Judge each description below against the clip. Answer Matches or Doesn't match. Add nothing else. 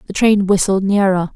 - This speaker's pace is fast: Doesn't match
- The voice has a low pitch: Doesn't match